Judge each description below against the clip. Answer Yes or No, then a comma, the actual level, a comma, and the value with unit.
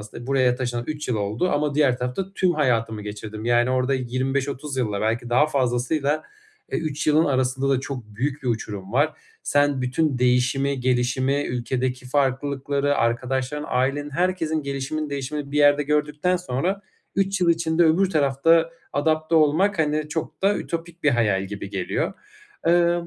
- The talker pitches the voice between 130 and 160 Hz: Yes, medium, 140 Hz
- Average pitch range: Yes, average, 3.7 semitones